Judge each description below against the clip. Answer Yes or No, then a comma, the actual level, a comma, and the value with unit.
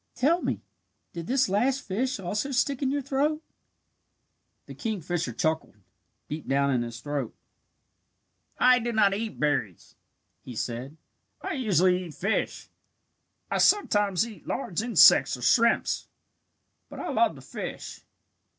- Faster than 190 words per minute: No, slow, 135 wpm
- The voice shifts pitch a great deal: Yes, wide, 8.8 semitones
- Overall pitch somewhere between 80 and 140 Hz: No, high, 200 Hz